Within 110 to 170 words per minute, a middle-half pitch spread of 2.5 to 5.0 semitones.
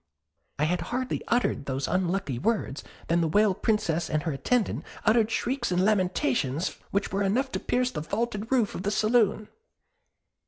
No: average, 165 wpm; wide, 5.4 semitones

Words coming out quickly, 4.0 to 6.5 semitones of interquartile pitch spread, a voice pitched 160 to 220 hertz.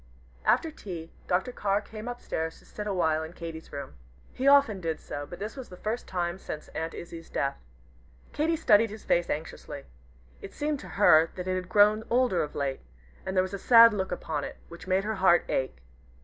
Yes: fast, 210 wpm; average, 4.7 semitones; medium, 185 Hz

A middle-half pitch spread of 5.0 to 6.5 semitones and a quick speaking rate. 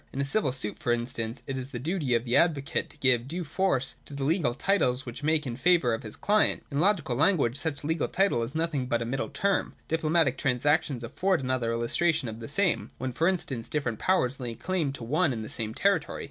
Yes: average, 5.3 semitones; fast, 230 wpm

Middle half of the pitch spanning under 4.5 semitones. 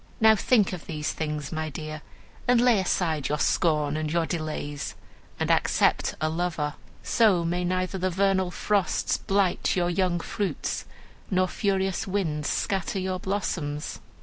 Yes: average, 3.7 semitones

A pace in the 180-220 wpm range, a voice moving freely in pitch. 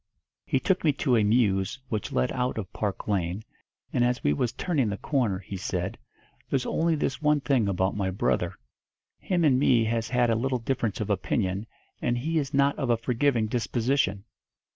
No: average, 190 wpm; average, 4.8 semitones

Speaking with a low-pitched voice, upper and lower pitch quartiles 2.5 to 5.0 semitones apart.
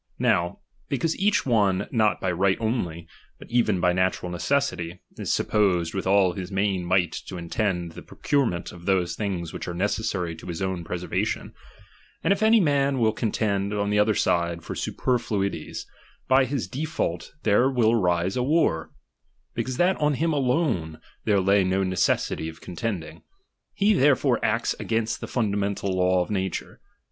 No: low, 100 Hz; wide, 5.5 semitones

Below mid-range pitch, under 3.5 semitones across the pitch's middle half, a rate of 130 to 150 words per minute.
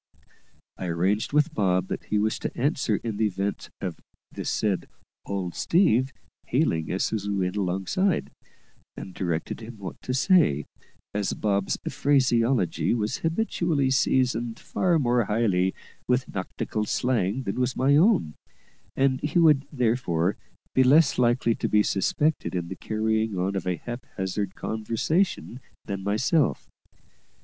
No: low, 110 Hz; wide, 5.4 semitones; average, 140 wpm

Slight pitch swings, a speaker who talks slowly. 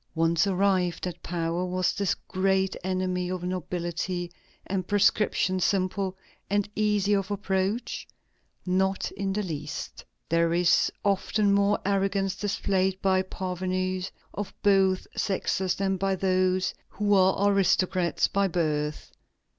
Yes: narrow, 1.5 semitones; slow, 125 wpm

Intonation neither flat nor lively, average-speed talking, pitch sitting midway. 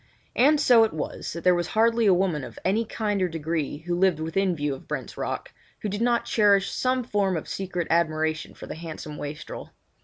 No: average, 5.0 semitones; fast, 210 wpm; medium, 180 Hz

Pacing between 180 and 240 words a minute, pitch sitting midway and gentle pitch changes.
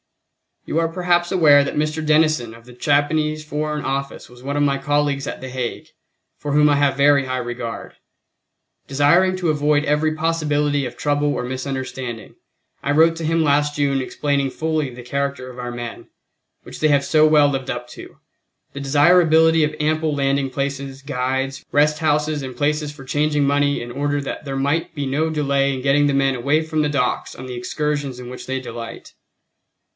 Yes: average, 190 wpm; medium, 145 Hz; narrow, 2.2 semitones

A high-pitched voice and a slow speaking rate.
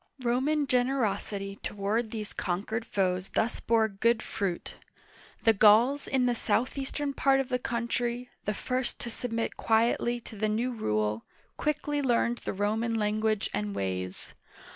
No: high, 225 Hz; average, 150 wpm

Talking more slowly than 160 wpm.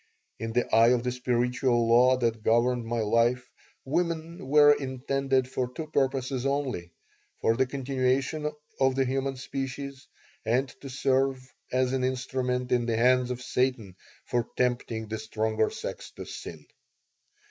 Yes: average, 145 wpm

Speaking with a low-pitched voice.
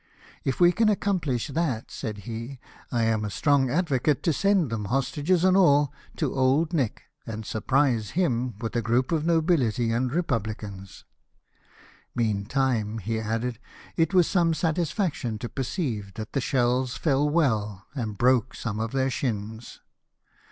Yes: low, 130 Hz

